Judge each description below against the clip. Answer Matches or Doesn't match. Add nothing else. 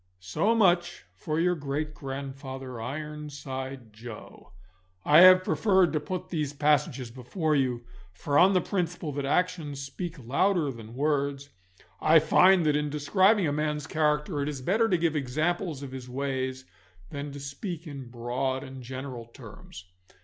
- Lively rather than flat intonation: Doesn't match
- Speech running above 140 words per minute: Matches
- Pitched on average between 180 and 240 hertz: Doesn't match